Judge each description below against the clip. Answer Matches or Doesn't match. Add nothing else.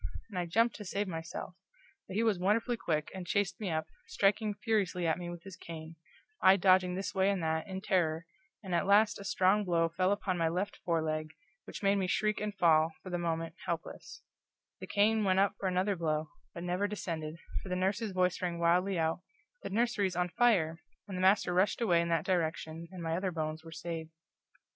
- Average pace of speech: Doesn't match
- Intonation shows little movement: Doesn't match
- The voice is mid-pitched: Matches